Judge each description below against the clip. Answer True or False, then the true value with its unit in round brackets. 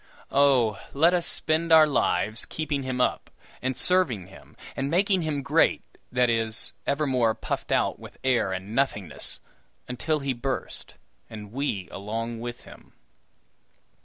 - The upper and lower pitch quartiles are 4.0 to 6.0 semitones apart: True (4.7 semitones)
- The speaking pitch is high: False (125 Hz)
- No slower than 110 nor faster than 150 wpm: True (140 wpm)